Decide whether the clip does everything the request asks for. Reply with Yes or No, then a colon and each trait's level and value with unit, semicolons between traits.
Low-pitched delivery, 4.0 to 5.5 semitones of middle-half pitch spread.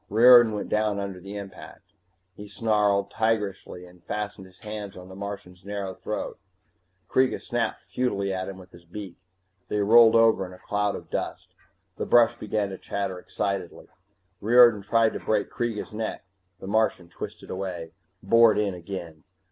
No: low, 100 Hz; narrow, 2.5 semitones